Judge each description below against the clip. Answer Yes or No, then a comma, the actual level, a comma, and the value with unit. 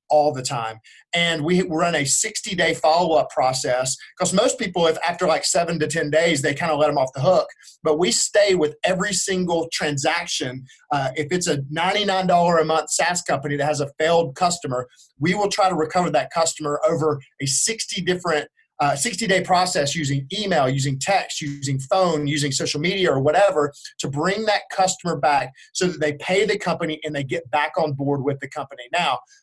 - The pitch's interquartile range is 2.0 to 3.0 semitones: No, average, 3.8 semitones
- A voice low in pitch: No, medium, 160 Hz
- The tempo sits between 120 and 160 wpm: No, average, 195 wpm